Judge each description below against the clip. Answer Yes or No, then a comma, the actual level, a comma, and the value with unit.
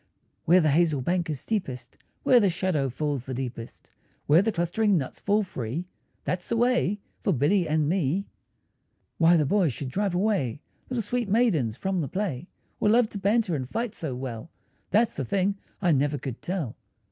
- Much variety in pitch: Yes, wide, 6.5 semitones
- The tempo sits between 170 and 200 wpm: Yes, average, 180 wpm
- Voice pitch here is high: No, medium, 175 Hz